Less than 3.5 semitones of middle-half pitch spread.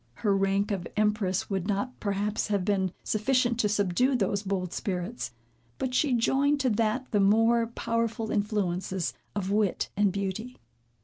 Yes: average, 2.9 semitones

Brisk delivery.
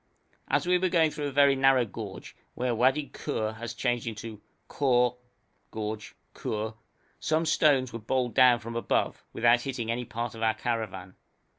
No: average, 165 wpm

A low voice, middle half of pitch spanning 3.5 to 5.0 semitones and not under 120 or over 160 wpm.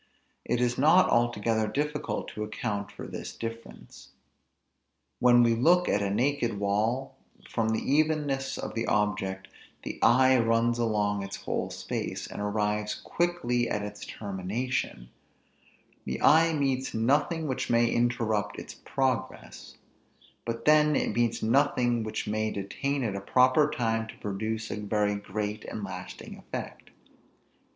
Yes: low, 115 Hz; average, 4.0 semitones; average, 140 wpm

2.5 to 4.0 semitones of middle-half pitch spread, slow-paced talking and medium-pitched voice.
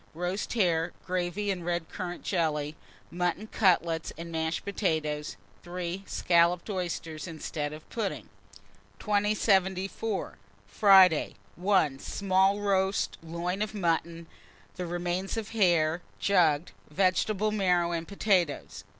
Yes: average, 2.8 semitones; slow, 110 wpm; medium, 180 Hz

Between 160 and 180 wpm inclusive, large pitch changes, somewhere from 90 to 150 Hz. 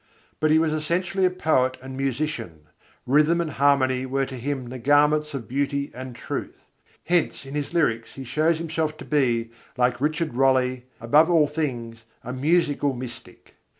No: average, 165 wpm; average, 3.3 semitones; medium, 140 Hz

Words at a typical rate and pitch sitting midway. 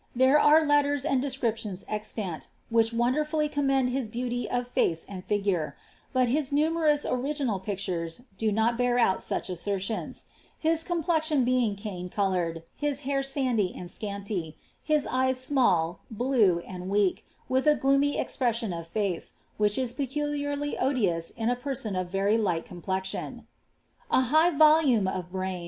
No: average, 155 wpm; high, 240 Hz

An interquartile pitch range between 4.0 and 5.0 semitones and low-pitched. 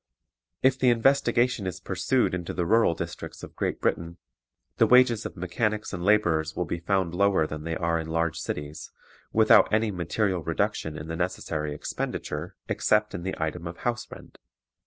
Yes: average, 4.5 semitones; very low, 90 Hz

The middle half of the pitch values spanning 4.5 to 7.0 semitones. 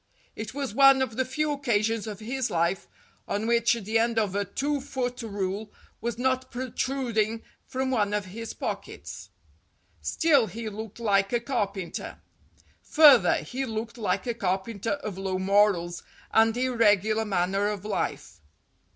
No: average, 3.8 semitones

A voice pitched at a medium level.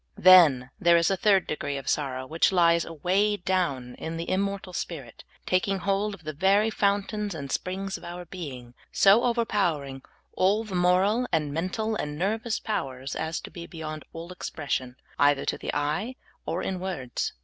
Yes: medium, 175 Hz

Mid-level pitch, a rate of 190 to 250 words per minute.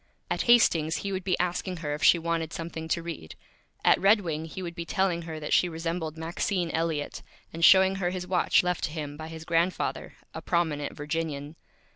Yes: medium, 165 Hz; average, 200 wpm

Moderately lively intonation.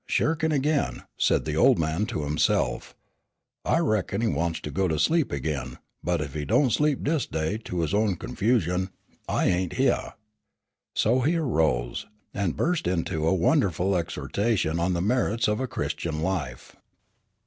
No: wide, 6.9 semitones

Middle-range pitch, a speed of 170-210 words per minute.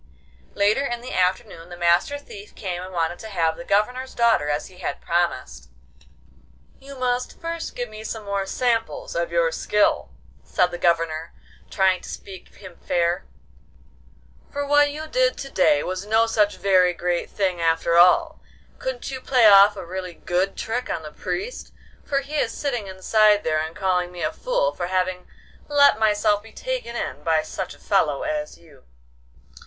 No: high, 200 Hz; average, 175 wpm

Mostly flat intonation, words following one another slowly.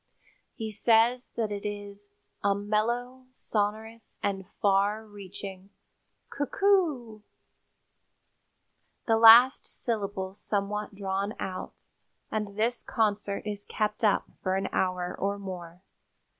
Yes: narrow, 2.1 semitones; slow, 115 wpm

